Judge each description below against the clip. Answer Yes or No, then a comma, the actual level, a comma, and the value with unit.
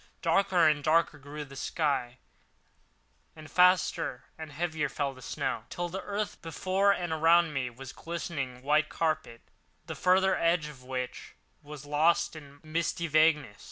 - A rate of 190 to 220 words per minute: No, average, 155 wpm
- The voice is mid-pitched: Yes, medium, 155 Hz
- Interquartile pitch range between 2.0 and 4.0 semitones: Yes, average, 3.1 semitones